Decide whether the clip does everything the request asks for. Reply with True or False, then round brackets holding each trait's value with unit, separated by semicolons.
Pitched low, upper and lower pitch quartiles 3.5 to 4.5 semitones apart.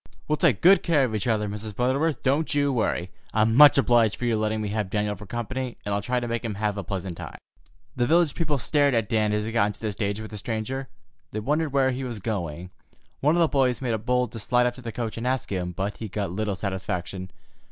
True (115 Hz; 4.1 semitones)